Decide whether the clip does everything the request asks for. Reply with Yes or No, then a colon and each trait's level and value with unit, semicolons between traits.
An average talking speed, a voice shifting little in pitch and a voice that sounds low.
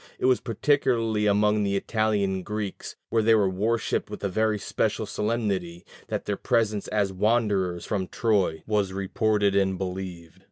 Yes: average, 150 wpm; narrow, 2.3 semitones; low, 105 Hz